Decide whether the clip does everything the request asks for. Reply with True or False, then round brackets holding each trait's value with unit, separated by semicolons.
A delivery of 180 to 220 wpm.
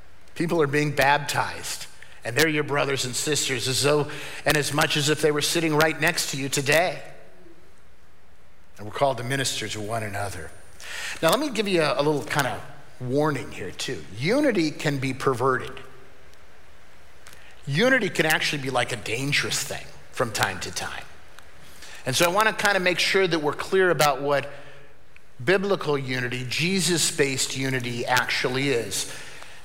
False (170 wpm)